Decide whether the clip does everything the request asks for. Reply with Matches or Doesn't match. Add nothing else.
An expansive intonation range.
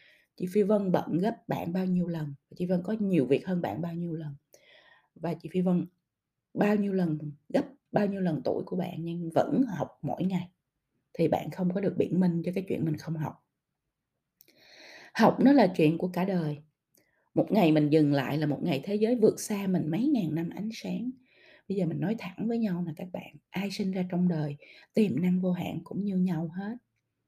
Doesn't match